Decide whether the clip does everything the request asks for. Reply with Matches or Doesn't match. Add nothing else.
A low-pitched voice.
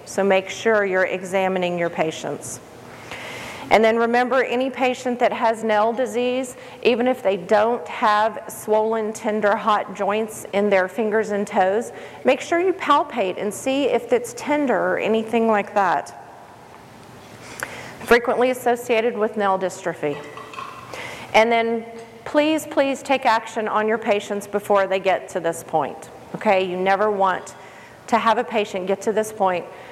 Doesn't match